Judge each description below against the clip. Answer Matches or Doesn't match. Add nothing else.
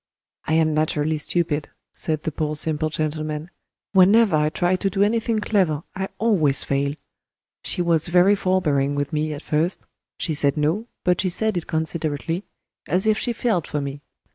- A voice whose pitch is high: Doesn't match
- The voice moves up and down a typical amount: Matches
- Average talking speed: Matches